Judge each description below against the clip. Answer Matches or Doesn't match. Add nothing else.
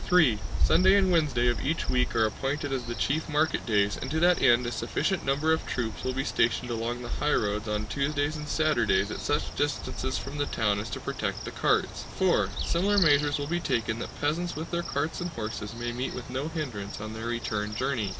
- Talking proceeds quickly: Matches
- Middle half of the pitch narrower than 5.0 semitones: Doesn't match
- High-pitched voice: Doesn't match